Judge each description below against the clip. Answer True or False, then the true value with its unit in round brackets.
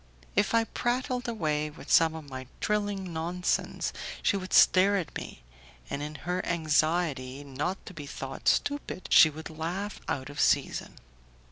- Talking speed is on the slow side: False (155 wpm)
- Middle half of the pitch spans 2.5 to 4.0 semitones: False (4.7 semitones)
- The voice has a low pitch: False (165 Hz)